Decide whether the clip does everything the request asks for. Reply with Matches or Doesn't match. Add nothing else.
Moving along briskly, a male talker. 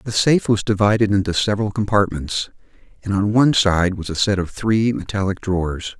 Doesn't match